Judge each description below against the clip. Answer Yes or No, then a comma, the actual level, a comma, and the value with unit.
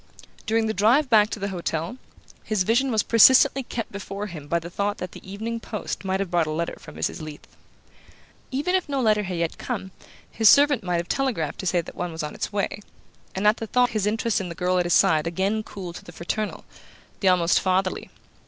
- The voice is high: Yes, high, 200 Hz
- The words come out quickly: Yes, fast, 225 wpm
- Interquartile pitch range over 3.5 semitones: Yes, average, 4.3 semitones